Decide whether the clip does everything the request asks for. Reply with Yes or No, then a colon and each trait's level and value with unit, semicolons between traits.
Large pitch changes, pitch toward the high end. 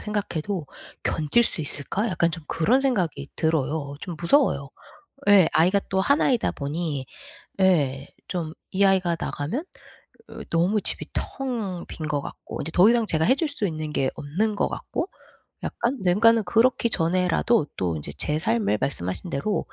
No: wide, 5.9 semitones; medium, 175 Hz